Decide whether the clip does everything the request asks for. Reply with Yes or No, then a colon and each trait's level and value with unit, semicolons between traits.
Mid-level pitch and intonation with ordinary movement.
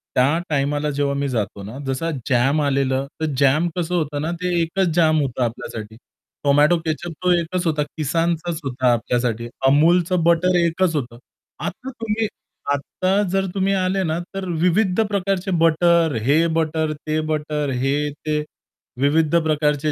Yes: medium, 155 Hz; average, 3.8 semitones